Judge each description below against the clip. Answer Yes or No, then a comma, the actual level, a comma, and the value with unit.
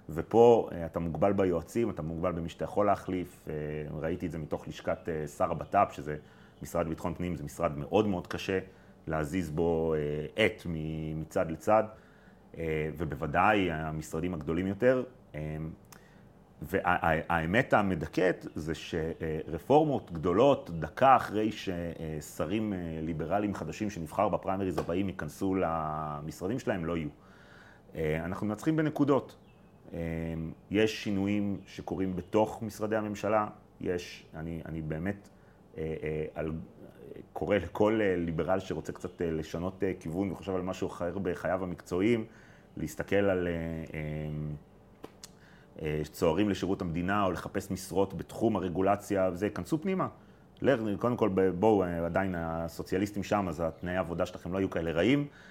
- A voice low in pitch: Yes, very low, 90 Hz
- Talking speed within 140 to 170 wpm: No, average, 115 wpm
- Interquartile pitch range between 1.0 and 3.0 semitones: No, average, 3.8 semitones